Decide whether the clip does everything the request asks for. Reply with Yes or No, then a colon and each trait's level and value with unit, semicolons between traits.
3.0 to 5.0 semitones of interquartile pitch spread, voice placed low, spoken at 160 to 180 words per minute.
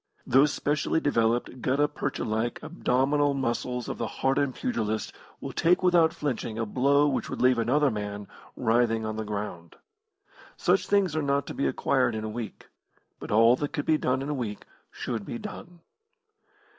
Yes: average, 4.6 semitones; low, 125 Hz; average, 175 wpm